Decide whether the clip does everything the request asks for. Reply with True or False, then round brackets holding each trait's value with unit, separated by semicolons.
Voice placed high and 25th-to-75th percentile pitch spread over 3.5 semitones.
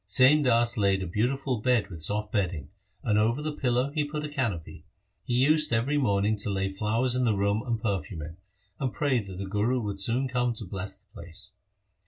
False (110 Hz; 4.5 semitones)